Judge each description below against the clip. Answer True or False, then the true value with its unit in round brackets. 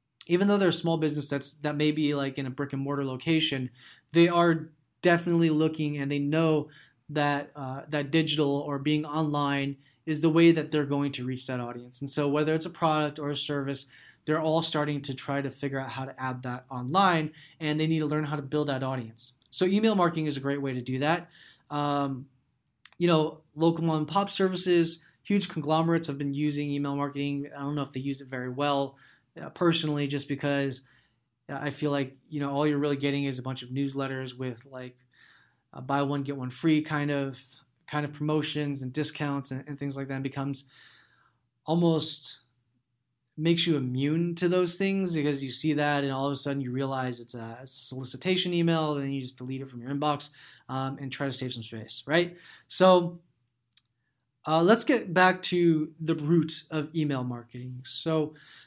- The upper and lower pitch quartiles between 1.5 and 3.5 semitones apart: True (2.8 semitones)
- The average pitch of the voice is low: False (145 Hz)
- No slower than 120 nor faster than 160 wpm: False (200 wpm)